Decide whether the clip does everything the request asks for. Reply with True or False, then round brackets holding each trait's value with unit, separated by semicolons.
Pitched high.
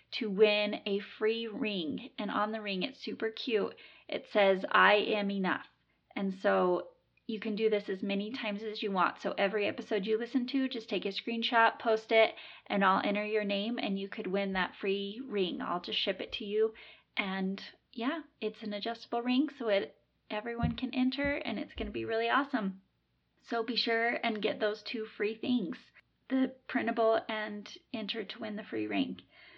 True (220 Hz)